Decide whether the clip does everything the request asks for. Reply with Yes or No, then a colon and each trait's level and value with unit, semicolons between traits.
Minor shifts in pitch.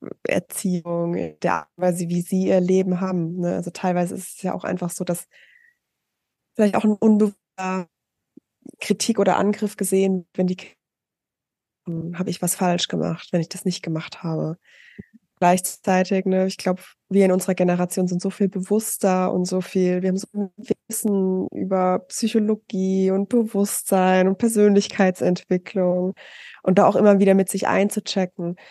Yes: narrow, 1.8 semitones